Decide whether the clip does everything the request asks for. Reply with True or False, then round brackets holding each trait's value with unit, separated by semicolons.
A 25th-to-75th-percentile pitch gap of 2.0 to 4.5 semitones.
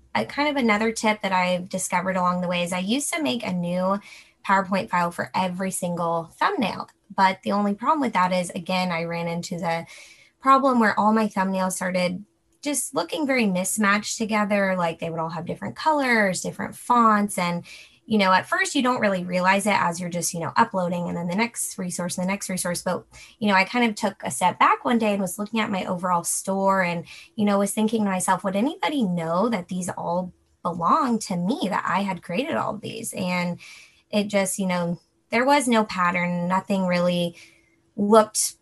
True (3.4 semitones)